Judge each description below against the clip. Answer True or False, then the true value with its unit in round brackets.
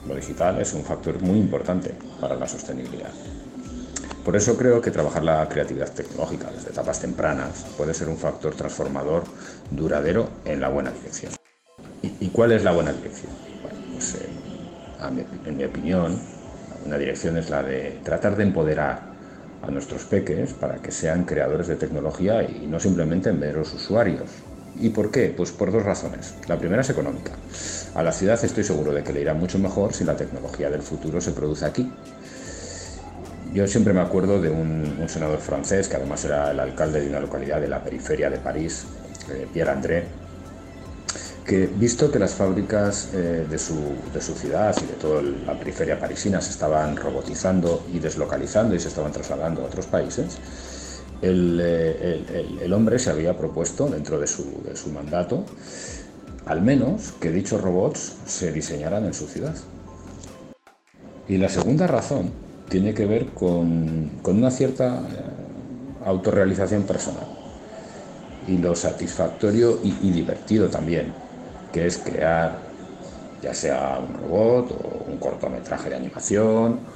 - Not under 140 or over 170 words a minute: True (160 wpm)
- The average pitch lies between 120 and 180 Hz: False (90 Hz)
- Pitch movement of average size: True (3.5 semitones)